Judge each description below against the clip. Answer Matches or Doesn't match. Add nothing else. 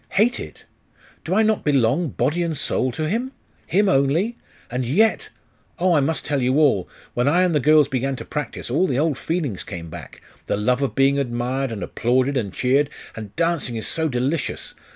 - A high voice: Doesn't match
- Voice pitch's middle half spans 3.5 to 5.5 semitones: Matches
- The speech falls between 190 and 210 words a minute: Matches